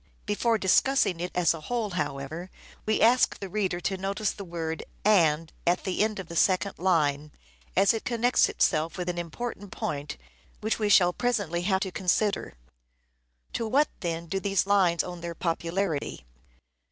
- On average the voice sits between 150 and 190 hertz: Yes, medium, 185 Hz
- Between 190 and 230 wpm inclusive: No, average, 175 wpm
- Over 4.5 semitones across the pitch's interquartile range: No, average, 3.6 semitones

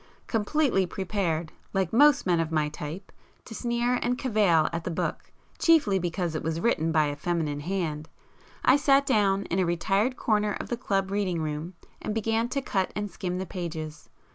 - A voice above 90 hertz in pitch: Yes, high, 190 Hz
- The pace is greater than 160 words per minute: Yes, average, 185 wpm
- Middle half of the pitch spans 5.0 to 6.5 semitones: Yes, average, 5.3 semitones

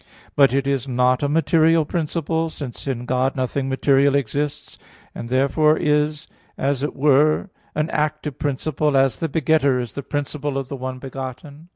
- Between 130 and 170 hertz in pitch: Yes, medium, 140 Hz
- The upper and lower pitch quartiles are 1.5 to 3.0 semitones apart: Yes, narrow, 2.4 semitones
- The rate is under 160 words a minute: No, average, 170 wpm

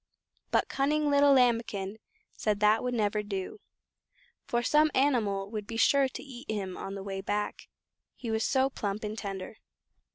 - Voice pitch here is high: Yes, high, 220 Hz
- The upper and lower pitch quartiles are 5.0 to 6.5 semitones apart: No, average, 4.4 semitones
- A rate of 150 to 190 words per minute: Yes, average, 165 wpm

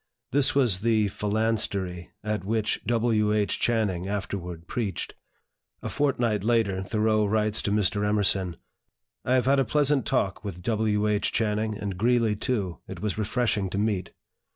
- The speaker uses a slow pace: No, average, 155 wpm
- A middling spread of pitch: No, narrow, 2.3 semitones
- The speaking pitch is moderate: No, low, 105 Hz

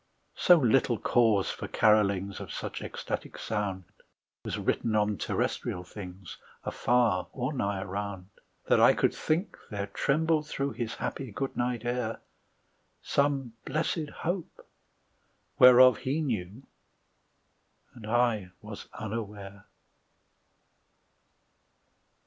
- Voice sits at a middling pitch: No, low, 115 Hz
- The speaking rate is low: Yes, slow, 110 wpm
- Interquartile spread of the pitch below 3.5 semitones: No, average, 4.6 semitones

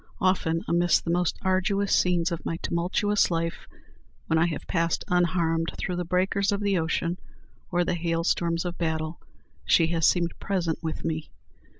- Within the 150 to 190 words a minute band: Yes, average, 170 wpm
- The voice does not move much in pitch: Yes, narrow, 1.5 semitones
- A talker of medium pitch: Yes, medium, 170 Hz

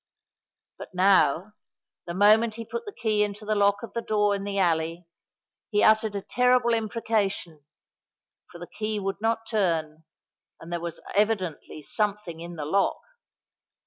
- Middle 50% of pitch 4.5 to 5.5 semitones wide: No, average, 4.0 semitones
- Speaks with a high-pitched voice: Yes, high, 200 Hz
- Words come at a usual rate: Yes, average, 150 wpm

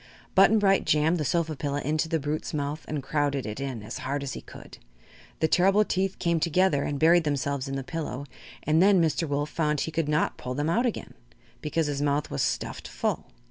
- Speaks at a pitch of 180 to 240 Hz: No, medium, 150 Hz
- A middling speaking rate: No, fast, 215 wpm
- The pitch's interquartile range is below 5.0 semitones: Yes, average, 2.9 semitones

